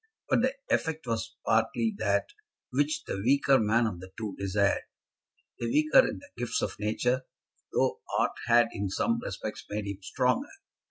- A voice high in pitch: No, low, 115 Hz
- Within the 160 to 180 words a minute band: Yes, average, 165 wpm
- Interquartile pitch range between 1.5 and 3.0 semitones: No, wide, 5.5 semitones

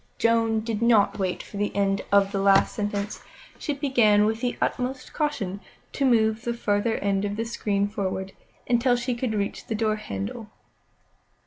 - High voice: Yes, high, 215 Hz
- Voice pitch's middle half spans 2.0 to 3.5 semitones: Yes, average, 2.8 semitones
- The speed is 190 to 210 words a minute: No, average, 175 wpm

